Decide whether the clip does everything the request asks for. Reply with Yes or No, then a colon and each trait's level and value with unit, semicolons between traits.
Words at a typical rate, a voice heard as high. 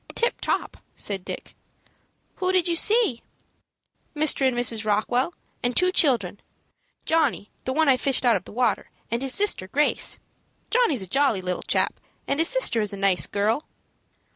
Yes: average, 165 wpm; very high, 255 Hz